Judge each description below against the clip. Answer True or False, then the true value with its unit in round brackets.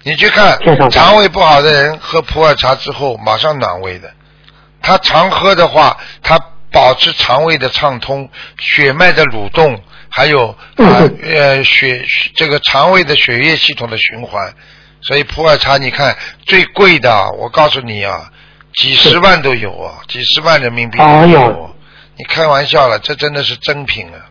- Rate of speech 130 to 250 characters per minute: True (240 characters per minute)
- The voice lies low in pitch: False (145 Hz)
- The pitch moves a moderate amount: True (4.1 semitones)